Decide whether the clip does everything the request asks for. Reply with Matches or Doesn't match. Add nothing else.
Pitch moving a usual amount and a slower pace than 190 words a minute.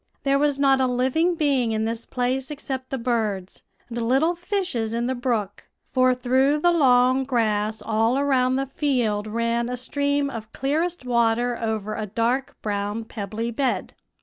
Matches